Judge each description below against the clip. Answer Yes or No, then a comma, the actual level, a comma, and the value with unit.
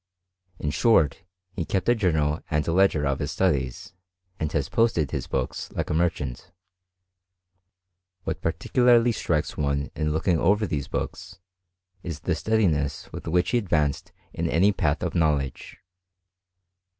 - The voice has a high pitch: No, very low, 80 Hz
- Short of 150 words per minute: Yes, average, 140 wpm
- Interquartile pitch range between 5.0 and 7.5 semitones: No, average, 4.6 semitones